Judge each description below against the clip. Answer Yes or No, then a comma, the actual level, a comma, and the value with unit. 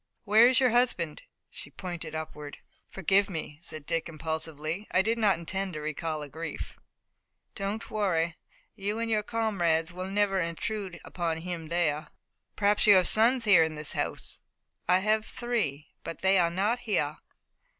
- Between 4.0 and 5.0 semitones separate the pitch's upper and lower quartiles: Yes, average, 4.6 semitones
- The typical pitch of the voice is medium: Yes, medium, 180 Hz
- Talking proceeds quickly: No, average, 160 wpm